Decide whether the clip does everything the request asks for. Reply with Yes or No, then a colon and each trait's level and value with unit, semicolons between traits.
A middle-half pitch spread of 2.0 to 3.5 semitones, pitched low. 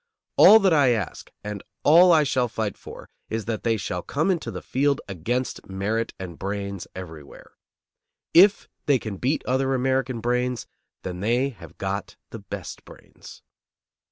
No: average, 5.3 semitones; low, 115 Hz